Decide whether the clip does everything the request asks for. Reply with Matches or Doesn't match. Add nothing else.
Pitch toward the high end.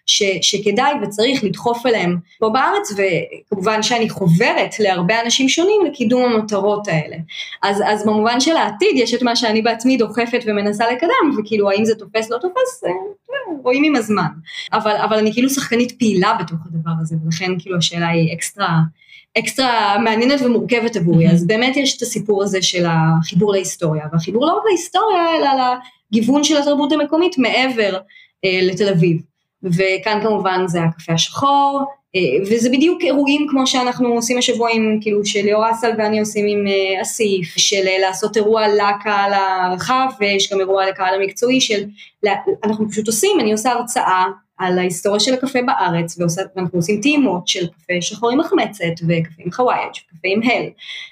Matches